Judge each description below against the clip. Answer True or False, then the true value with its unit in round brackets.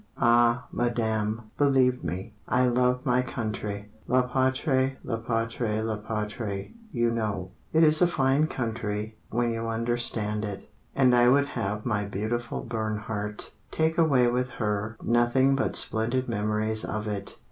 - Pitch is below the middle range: True (115 Hz)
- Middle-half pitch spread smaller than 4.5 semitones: True (2.9 semitones)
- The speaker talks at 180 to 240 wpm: False (145 wpm)